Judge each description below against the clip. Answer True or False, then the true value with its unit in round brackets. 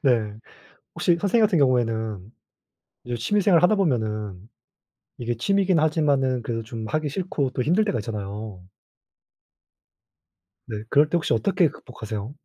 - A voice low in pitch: True (125 Hz)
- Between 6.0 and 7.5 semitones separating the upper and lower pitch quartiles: True (6.8 semitones)